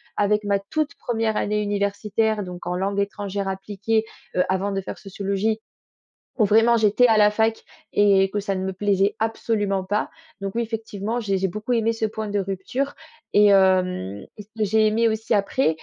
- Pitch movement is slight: Yes, narrow, 2.1 semitones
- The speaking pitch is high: Yes, high, 205 Hz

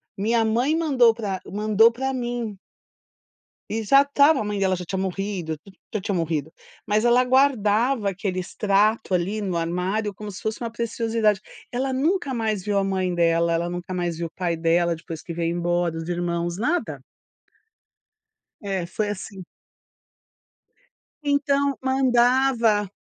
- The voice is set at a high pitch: Yes, high, 205 Hz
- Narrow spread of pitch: No, average, 5.2 semitones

